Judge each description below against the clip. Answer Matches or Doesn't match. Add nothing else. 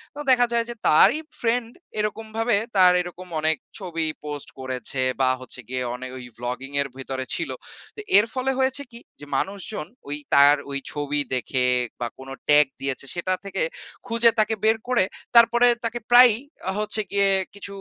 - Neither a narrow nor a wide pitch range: Doesn't match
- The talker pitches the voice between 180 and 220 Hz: Matches